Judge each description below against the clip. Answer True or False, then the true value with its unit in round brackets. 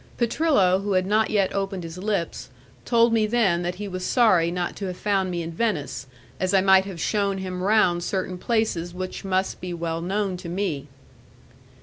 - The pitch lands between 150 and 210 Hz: True (190 Hz)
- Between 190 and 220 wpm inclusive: True (195 wpm)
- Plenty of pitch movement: False (2.7 semitones)